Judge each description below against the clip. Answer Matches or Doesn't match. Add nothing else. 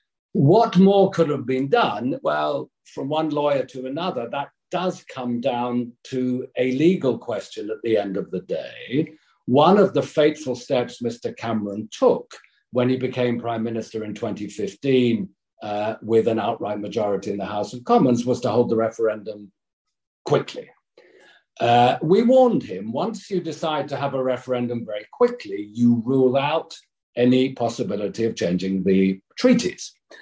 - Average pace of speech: Matches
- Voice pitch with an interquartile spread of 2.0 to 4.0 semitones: Doesn't match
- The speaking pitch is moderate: Doesn't match